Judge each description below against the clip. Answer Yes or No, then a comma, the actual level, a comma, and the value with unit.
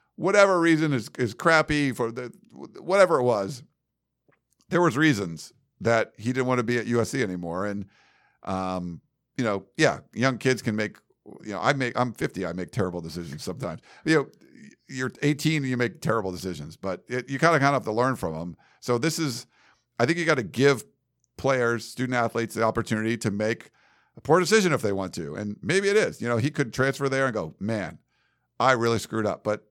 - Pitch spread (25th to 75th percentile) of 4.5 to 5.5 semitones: Yes, average, 4.8 semitones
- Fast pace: Yes, fast, 210 wpm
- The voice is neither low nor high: No, low, 120 Hz